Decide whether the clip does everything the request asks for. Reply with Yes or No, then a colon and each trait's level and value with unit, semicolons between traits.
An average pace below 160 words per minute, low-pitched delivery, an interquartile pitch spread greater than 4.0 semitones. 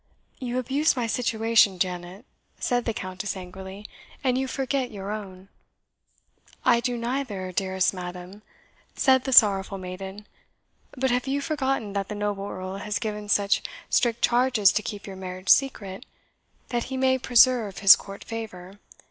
No: average, 150 wpm; high, 210 Hz; average, 4.5 semitones